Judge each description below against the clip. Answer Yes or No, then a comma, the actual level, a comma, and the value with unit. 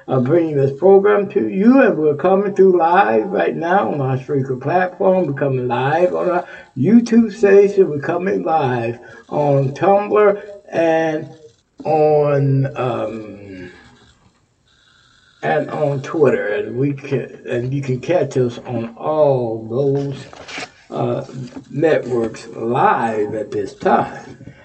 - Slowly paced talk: Yes, slow, 125 wpm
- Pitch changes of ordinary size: No, wide, 6.3 semitones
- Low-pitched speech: No, medium, 145 Hz